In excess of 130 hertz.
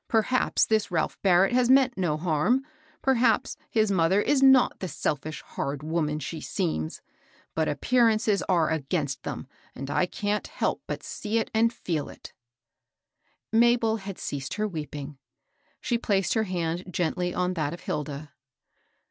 Yes: medium, 185 Hz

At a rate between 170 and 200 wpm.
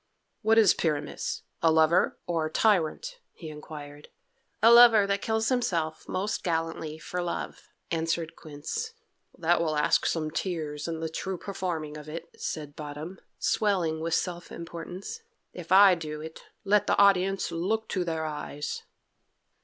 No: average, 150 wpm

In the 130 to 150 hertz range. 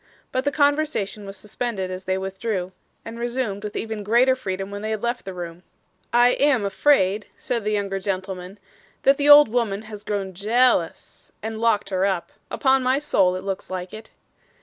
No: high, 210 Hz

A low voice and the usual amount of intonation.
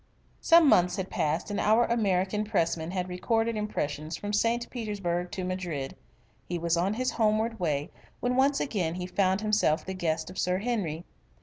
No: high, 190 Hz; average, 4.1 semitones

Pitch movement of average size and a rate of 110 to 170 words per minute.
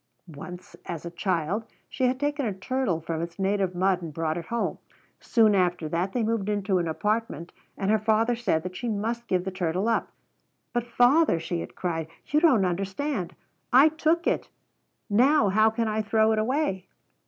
No: average, 4.9 semitones; average, 190 wpm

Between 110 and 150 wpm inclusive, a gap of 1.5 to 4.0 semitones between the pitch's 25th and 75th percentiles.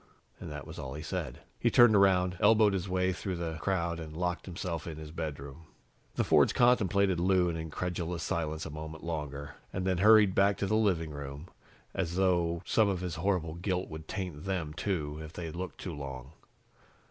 No: average, 195 wpm; average, 3.3 semitones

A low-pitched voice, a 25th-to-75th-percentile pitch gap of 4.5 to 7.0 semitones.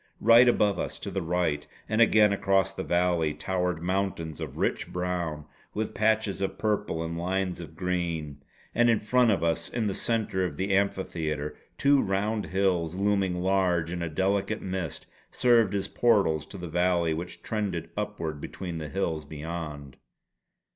No: very low, 90 Hz; average, 3.4 semitones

